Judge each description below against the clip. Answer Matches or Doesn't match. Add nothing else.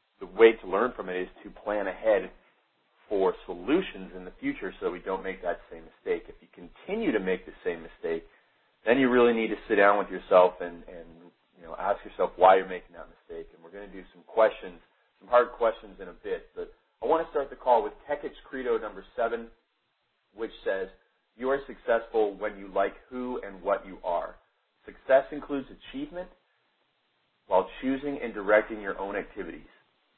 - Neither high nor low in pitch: Doesn't match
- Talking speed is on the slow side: Doesn't match